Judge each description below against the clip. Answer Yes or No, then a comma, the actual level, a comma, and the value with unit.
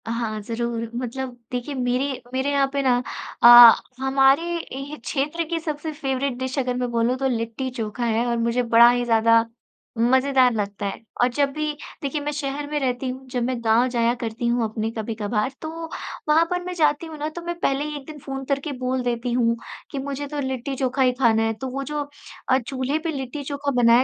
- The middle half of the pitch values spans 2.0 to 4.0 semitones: Yes, average, 3.1 semitones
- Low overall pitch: No, very high, 260 Hz